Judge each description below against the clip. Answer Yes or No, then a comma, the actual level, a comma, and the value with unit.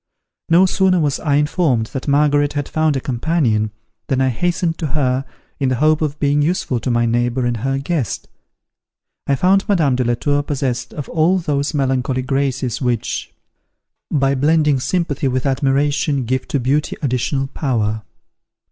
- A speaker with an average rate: Yes, average, 165 wpm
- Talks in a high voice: No, medium, 140 Hz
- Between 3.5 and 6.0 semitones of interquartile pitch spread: No, average, 3.0 semitones